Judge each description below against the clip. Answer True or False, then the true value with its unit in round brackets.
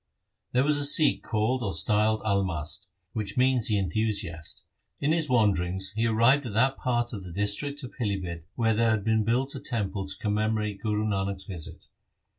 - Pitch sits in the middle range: False (110 Hz)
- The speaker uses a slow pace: False (180 wpm)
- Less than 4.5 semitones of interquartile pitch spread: True (3.6 semitones)